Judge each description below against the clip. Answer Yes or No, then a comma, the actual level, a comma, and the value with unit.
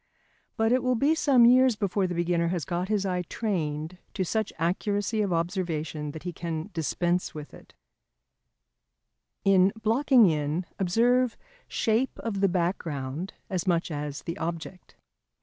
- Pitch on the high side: No, medium, 180 Hz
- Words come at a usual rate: Yes, average, 150 wpm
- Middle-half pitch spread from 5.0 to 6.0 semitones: No, average, 4.6 semitones